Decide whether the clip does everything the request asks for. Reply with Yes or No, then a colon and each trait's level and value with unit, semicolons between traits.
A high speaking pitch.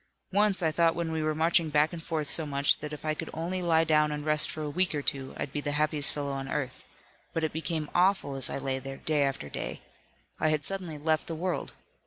No: medium, 155 Hz